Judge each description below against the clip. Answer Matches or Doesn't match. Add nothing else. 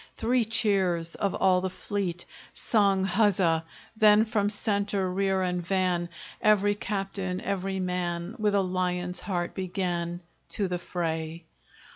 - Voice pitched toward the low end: Doesn't match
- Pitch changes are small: Matches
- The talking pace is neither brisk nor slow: Doesn't match